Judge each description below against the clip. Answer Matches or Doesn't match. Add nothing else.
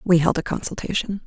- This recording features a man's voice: Doesn't match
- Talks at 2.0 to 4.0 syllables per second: Doesn't match